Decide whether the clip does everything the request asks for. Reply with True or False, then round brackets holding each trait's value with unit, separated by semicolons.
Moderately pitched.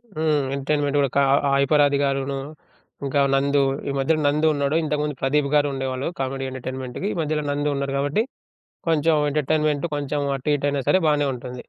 True (145 Hz)